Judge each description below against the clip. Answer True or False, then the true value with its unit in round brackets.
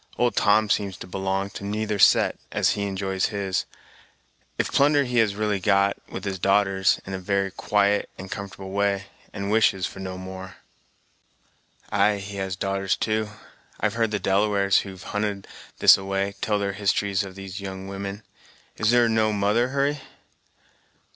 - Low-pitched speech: True (100 Hz)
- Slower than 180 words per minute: True (165 wpm)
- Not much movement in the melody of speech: True (1.6 semitones)